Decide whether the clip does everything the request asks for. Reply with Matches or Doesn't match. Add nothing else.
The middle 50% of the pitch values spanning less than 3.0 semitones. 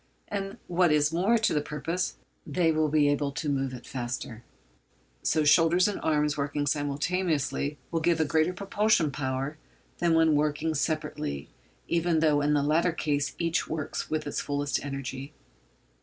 Matches